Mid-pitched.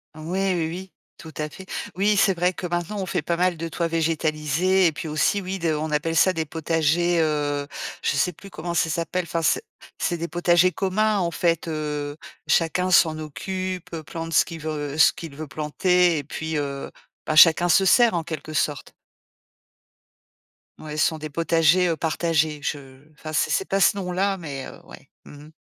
Yes: medium, 165 Hz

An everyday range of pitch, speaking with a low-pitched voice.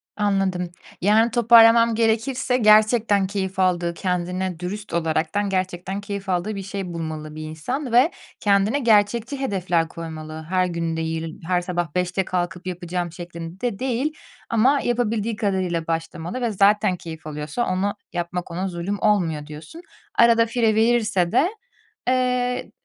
No: average, 4.7 semitones; high, 190 Hz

